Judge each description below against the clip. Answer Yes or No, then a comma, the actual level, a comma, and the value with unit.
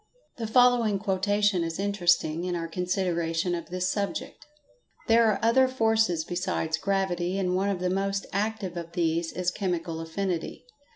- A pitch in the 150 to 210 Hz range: Yes, medium, 185 Hz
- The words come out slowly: No, average, 155 wpm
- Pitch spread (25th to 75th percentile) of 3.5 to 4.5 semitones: No, average, 2.9 semitones